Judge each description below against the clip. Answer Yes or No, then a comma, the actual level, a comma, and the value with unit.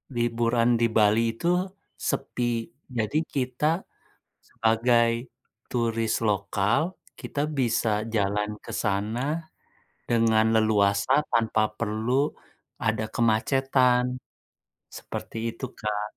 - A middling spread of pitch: No, narrow, 2.2 semitones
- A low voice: Yes, low, 115 Hz